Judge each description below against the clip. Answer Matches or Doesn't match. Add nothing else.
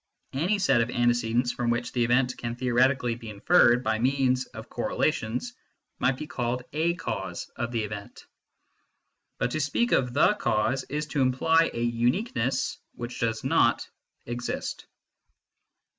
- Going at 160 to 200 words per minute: Doesn't match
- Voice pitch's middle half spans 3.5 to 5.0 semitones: Doesn't match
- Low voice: Matches